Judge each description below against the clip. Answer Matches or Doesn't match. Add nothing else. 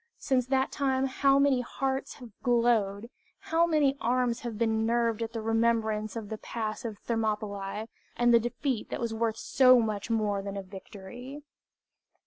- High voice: Matches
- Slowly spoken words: Doesn't match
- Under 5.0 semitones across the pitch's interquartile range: Matches